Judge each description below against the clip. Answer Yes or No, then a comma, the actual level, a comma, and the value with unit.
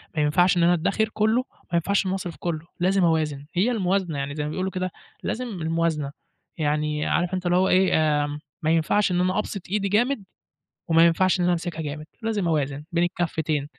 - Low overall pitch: No, medium, 175 Hz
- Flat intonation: No, average, 3.5 semitones